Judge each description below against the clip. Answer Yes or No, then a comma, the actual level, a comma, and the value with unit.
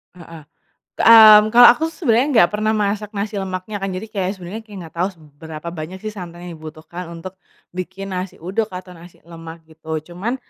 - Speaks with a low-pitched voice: No, medium, 185 Hz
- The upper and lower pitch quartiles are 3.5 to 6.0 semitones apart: Yes, average, 3.9 semitones